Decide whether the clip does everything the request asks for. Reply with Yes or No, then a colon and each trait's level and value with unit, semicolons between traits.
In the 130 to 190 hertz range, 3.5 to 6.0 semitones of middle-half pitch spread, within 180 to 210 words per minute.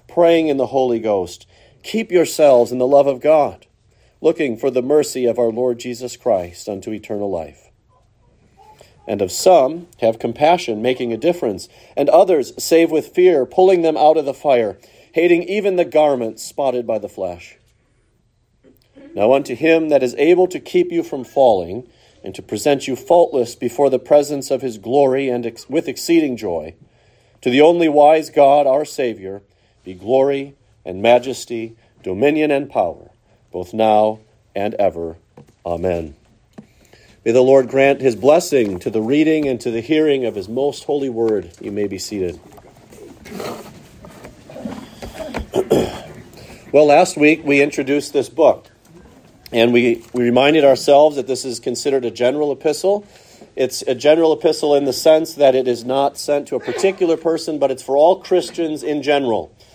No: low, 135 Hz; average, 4.5 semitones; average, 160 wpm